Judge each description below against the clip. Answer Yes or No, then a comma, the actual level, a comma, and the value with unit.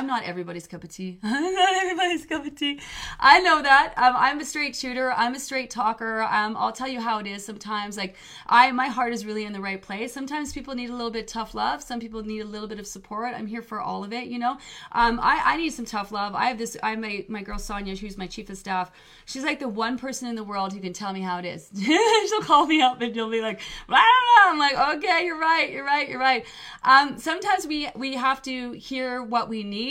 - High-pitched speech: Yes, high, 240 Hz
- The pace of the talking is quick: Yes, fast, 265 wpm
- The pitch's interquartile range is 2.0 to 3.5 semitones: No, average, 4.7 semitones